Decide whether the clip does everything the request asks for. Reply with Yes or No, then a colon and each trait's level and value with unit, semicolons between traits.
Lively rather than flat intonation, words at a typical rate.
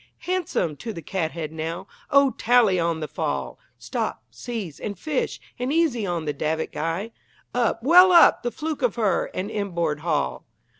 Yes: wide, 7.2 semitones; average, 165 wpm